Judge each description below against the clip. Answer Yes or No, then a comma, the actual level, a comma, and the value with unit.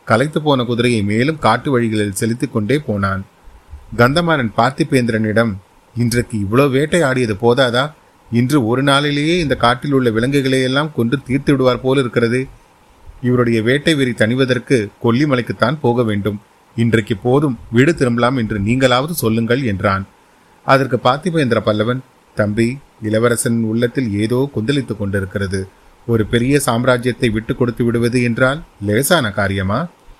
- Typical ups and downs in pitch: Yes, average, 3.1 semitones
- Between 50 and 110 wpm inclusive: No, average, 120 wpm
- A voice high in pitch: No, low, 120 Hz